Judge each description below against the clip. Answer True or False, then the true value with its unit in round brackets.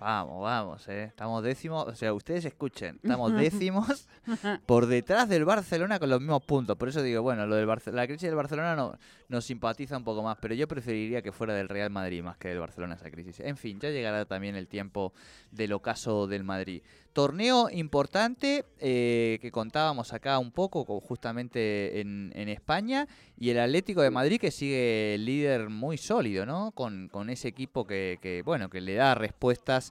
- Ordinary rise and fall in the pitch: False (5.7 semitones)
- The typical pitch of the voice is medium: False (120 Hz)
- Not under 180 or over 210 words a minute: True (190 wpm)